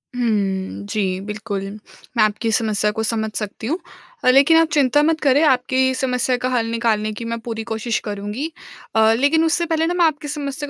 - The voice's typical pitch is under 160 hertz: No, high, 245 Hz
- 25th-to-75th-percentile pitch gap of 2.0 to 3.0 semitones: No, average, 4.9 semitones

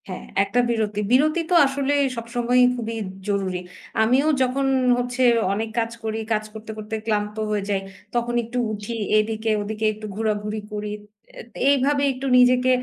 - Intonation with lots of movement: No, average, 2.9 semitones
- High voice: Yes, high, 225 Hz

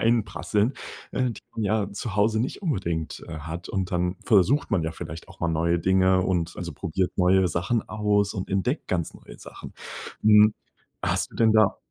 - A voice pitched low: Yes, very low, 95 Hz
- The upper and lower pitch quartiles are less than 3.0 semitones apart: No, average, 3.6 semitones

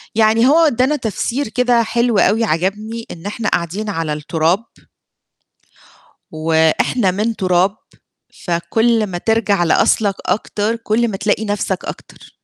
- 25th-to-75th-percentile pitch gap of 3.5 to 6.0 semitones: Yes, average, 4.2 semitones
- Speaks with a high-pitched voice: Yes, high, 210 Hz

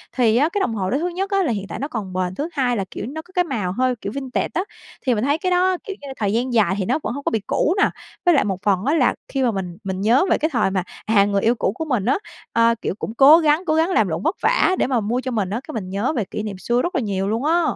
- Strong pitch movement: Yes, wide, 7.2 semitones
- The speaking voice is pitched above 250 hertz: No, high, 245 Hz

